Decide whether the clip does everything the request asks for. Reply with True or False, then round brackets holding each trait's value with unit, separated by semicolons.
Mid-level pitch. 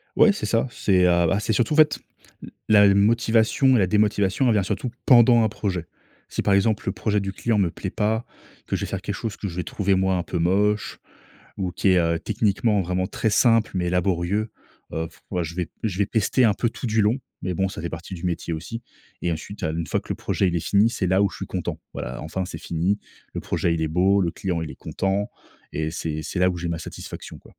False (95 Hz)